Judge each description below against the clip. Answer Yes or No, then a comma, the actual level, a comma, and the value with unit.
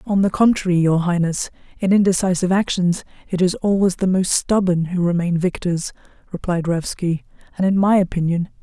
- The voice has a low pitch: No, medium, 180 Hz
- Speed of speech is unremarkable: Yes, average, 160 wpm